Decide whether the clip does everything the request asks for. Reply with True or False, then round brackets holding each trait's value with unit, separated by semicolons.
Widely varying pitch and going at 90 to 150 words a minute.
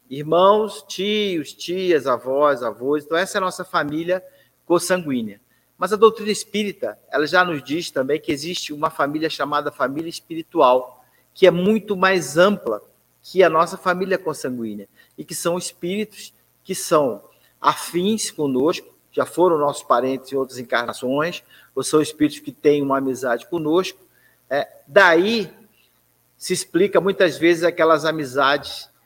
False (4.9 semitones; 140 wpm)